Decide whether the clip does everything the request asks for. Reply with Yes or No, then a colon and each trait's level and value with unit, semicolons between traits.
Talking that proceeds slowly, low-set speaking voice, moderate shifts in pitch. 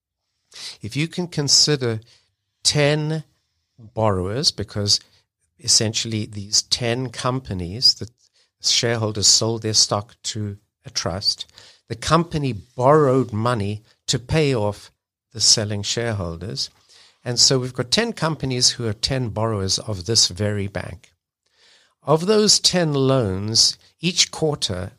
Yes: slow, 120 wpm; low, 115 Hz; average, 4.7 semitones